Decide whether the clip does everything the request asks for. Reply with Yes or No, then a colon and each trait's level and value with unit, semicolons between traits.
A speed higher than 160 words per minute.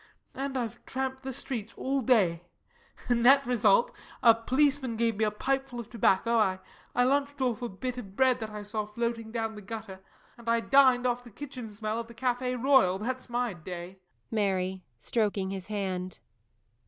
Yes: average, 175 wpm